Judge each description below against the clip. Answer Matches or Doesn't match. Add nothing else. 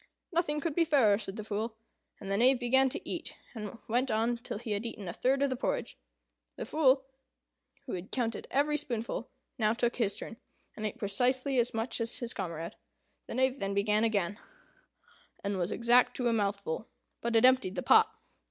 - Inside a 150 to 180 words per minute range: Doesn't match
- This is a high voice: Matches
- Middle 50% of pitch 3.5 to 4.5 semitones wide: Matches